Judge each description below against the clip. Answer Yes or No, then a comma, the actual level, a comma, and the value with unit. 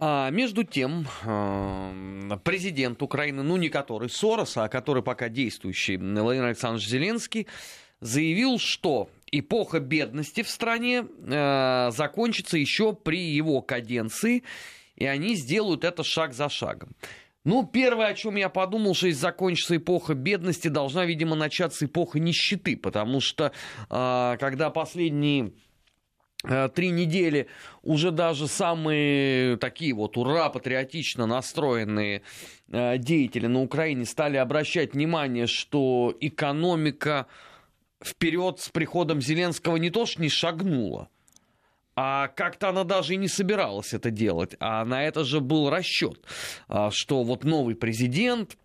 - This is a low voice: No, medium, 150 Hz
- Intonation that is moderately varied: No, wide, 5.7 semitones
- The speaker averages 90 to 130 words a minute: Yes, average, 125 wpm